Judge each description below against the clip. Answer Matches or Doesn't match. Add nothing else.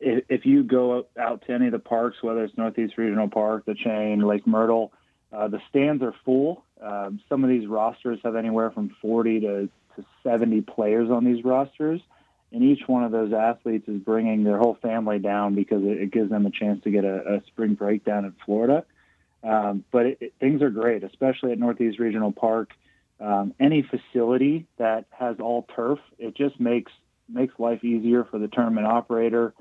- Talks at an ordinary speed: Matches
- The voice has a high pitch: Doesn't match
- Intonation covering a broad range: Doesn't match